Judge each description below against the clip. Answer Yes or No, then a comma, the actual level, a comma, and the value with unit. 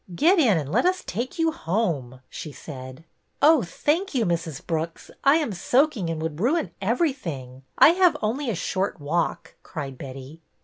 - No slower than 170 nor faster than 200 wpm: Yes, average, 175 wpm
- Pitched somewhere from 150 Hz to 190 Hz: Yes, medium, 185 Hz